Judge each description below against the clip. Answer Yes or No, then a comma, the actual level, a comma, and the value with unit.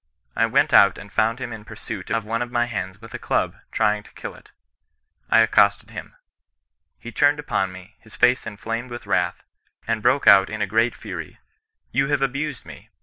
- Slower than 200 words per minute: No, fast, 205 wpm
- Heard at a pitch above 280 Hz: No, low, 115 Hz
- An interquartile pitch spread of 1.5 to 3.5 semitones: Yes, average, 3.1 semitones